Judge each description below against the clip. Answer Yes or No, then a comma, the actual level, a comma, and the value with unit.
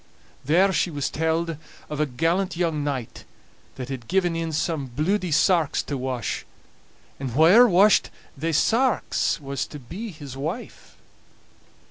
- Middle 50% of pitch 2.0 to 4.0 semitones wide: No, average, 4.5 semitones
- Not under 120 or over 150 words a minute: Yes, average, 140 wpm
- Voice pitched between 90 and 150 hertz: No, medium, 160 Hz